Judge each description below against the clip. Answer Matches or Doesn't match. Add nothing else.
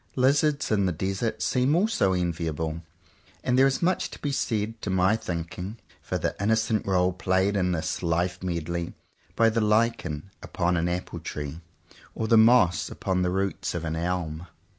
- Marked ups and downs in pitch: Doesn't match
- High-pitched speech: Doesn't match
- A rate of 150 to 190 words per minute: Matches